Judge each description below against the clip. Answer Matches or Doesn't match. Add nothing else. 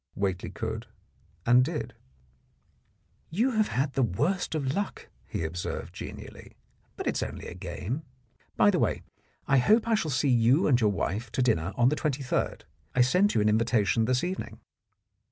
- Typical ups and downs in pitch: Doesn't match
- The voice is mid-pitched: Doesn't match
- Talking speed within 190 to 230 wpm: Doesn't match